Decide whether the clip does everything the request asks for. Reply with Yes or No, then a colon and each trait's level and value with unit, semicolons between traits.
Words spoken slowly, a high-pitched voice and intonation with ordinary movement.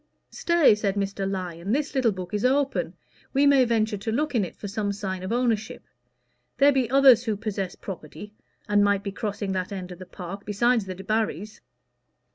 No: average, 190 wpm; high, 210 Hz; average, 3.8 semitones